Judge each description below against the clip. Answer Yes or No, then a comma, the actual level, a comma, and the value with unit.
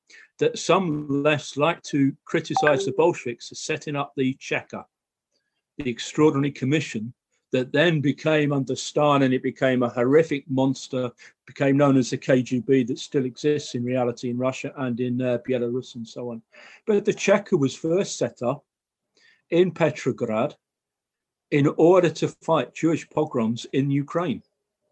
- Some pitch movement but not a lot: Yes, average, 3.3 semitones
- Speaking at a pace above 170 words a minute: No, average, 150 wpm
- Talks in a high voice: No, medium, 140 Hz